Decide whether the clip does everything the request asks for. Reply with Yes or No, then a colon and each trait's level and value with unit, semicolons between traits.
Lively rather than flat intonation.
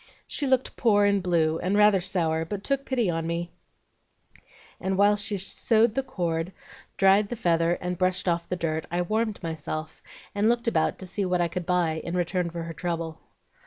No: average, 3.5 semitones